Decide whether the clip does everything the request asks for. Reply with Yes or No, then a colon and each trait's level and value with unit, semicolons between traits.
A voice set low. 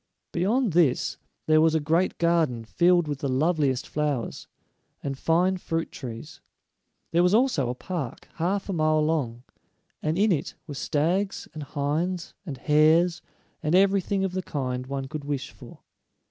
No: medium, 155 Hz